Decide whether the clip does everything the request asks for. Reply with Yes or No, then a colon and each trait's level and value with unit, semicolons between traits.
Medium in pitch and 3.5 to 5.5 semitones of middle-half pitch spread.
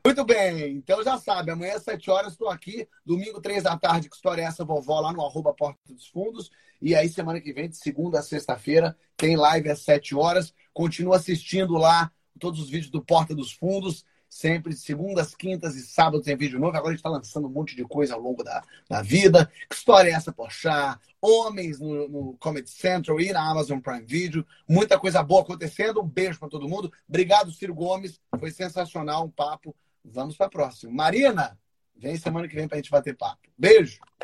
Yes: medium, 165 Hz; average, 3.9 semitones